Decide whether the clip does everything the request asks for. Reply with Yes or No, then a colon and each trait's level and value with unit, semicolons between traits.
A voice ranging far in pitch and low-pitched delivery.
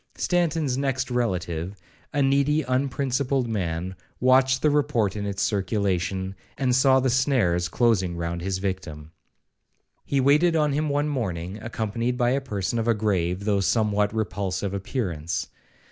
Yes: wide, 6.0 semitones; low, 110 Hz